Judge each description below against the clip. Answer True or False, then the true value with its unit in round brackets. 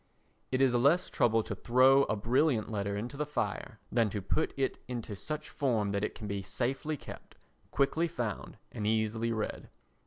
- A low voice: True (120 Hz)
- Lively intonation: False (4.4 semitones)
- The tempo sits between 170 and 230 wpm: True (180 wpm)